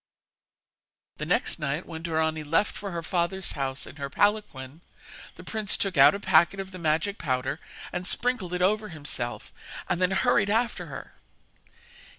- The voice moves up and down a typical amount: Yes, average, 4.6 semitones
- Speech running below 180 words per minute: Yes, average, 160 wpm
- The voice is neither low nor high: Yes, medium, 175 Hz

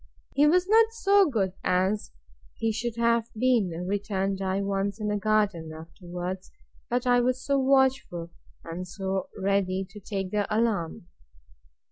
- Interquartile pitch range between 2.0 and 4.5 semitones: Yes, average, 4.2 semitones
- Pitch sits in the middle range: No, high, 205 Hz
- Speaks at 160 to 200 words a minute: No, average, 145 wpm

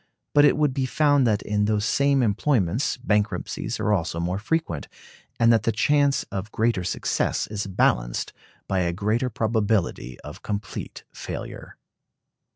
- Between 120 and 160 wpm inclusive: Yes, average, 150 wpm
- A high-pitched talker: No, low, 110 Hz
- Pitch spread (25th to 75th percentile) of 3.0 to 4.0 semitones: No, average, 4.7 semitones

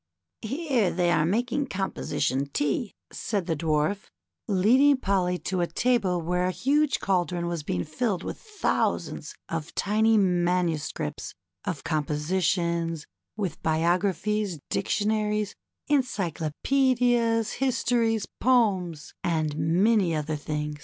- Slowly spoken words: Yes, slow, 115 wpm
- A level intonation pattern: No, wide, 5.4 semitones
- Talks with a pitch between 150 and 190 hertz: Yes, medium, 185 Hz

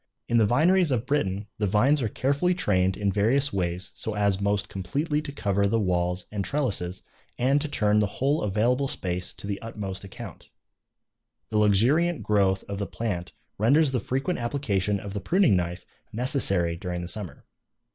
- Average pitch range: No, wide, 5.9 semitones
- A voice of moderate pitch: No, low, 105 Hz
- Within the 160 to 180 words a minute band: Yes, average, 175 wpm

